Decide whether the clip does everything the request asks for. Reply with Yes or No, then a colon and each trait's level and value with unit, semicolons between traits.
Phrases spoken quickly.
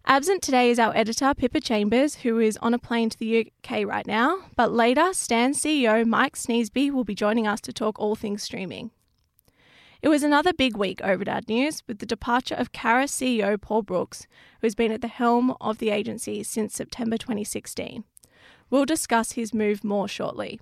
No: average, 195 wpm